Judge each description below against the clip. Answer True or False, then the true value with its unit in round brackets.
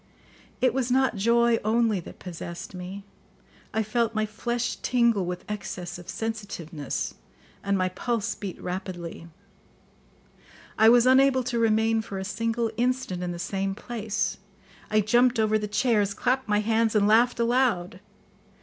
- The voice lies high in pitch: True (220 Hz)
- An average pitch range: True (3.4 semitones)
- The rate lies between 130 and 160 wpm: True (150 wpm)